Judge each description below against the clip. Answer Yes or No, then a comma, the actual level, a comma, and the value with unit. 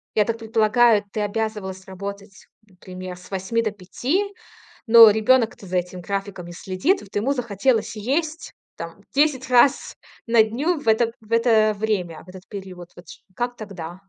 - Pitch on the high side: Yes, high, 215 Hz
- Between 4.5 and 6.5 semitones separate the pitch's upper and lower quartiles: No, average, 3.9 semitones